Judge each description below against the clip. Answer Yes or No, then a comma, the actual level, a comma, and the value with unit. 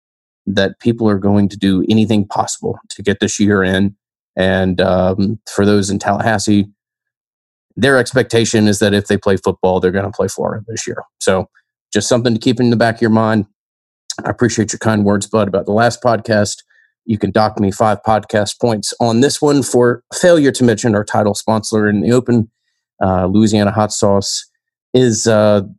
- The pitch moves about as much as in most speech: No, narrow, 2.3 semitones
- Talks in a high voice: No, low, 105 Hz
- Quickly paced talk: No, average, 190 wpm